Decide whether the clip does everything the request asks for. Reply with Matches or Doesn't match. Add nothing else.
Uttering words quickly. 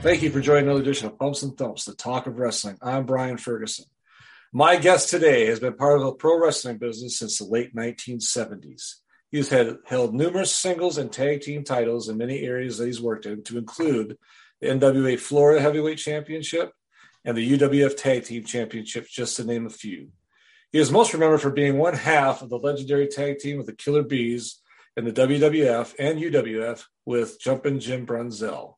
Doesn't match